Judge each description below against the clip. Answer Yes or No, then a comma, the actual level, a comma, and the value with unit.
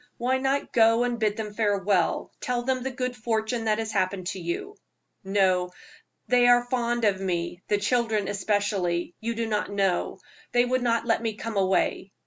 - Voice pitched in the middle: No, high, 220 Hz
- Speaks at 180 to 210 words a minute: Yes, average, 185 wpm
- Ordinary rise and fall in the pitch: Yes, average, 3.7 semitones